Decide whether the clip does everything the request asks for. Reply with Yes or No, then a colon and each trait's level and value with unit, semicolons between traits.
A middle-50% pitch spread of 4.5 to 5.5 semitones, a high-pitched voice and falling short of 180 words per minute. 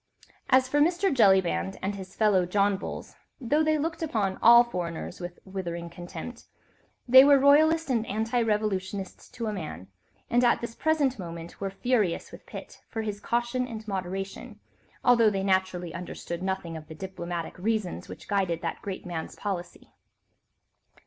Yes: average, 5.1 semitones; high, 200 Hz; average, 160 wpm